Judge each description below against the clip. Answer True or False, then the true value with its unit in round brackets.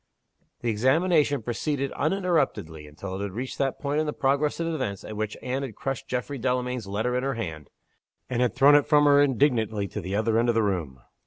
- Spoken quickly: True (215 wpm)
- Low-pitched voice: True (125 Hz)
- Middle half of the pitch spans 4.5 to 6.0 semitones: True (5.1 semitones)